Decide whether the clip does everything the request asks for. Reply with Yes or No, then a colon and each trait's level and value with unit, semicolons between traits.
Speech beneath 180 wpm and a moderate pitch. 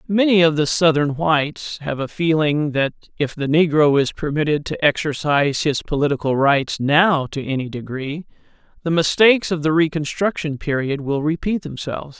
Yes: average, 160 wpm; medium, 150 Hz